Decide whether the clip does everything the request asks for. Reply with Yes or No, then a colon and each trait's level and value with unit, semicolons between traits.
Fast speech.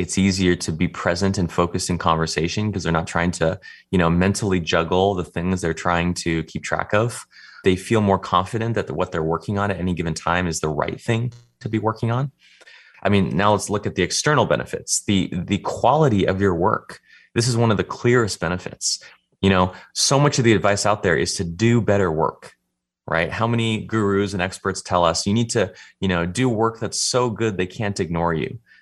Yes: fast, 220 wpm